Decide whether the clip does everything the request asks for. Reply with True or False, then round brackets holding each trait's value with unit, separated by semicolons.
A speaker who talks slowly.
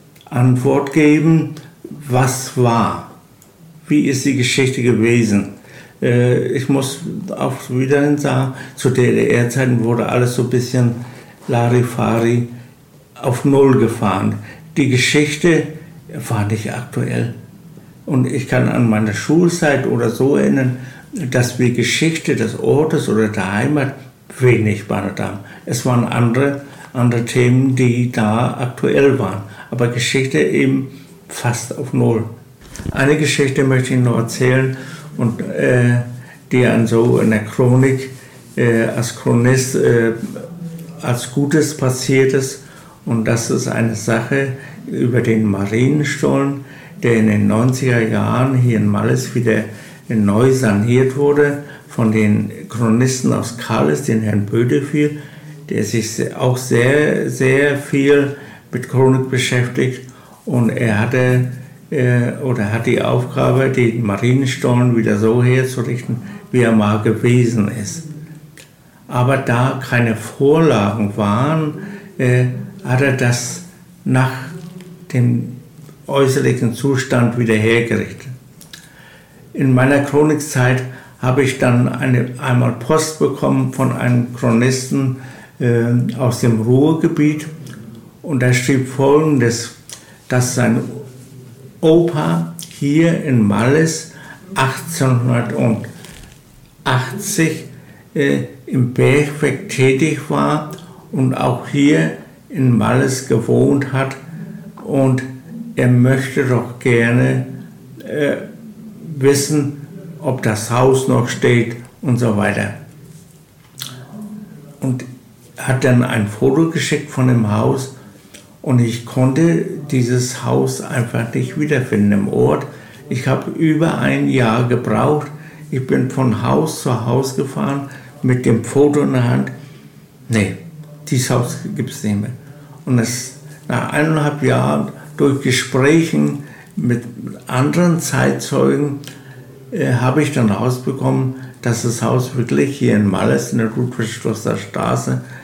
True (115 wpm)